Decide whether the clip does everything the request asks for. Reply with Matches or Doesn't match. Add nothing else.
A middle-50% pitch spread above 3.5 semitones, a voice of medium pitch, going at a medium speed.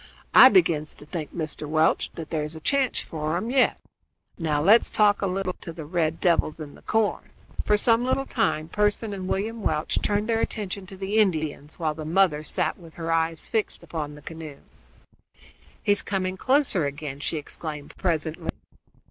Matches